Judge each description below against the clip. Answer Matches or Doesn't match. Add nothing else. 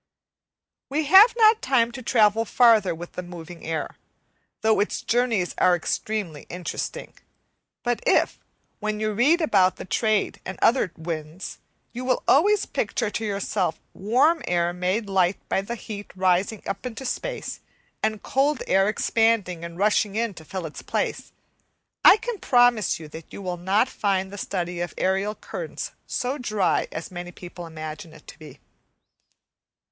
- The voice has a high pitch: Matches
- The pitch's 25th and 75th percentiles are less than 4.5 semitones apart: Doesn't match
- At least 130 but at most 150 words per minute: Doesn't match